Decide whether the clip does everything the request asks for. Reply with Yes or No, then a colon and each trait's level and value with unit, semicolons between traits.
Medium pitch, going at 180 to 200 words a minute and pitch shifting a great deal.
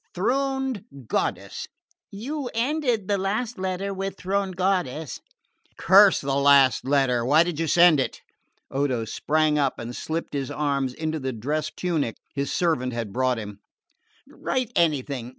No: medium, 155 Hz; average, 150 wpm; wide, 6.4 semitones